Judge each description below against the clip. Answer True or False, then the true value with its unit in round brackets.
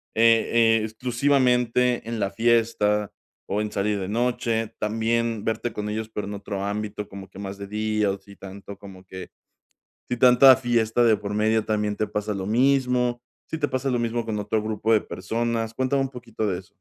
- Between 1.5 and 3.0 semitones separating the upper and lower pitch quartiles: True (2.5 semitones)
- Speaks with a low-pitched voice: True (110 Hz)